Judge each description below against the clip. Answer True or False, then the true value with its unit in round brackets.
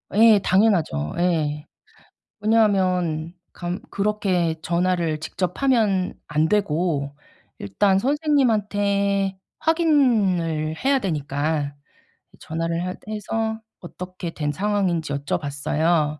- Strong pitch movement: False (4.8 semitones)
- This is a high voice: False (180 Hz)